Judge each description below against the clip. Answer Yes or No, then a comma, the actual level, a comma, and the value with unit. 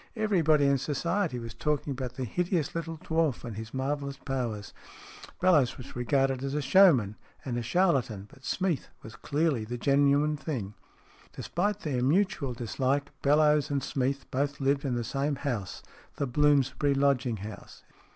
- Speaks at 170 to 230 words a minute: No, average, 160 wpm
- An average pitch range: Yes, average, 3.3 semitones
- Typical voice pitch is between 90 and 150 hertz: Yes, medium, 140 Hz